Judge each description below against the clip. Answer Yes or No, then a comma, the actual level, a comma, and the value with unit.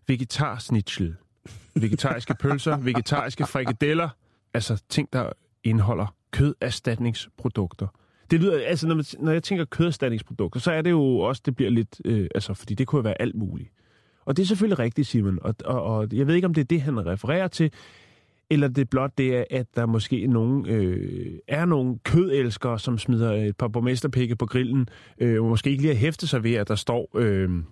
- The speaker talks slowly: No, average, 190 wpm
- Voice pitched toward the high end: No, low, 125 Hz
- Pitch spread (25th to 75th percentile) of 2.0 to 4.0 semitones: No, average, 4.5 semitones